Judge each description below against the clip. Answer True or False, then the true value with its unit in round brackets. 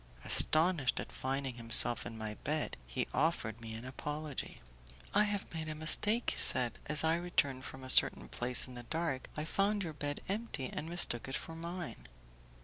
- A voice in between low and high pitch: True (150 Hz)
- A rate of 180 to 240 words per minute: True (185 wpm)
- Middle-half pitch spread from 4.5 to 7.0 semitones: True (4.9 semitones)